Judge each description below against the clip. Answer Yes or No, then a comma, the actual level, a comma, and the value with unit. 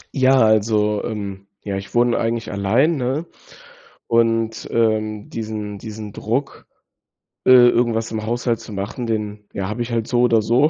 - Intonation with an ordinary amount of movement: No, narrow, 2.2 semitones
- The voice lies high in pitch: No, low, 115 Hz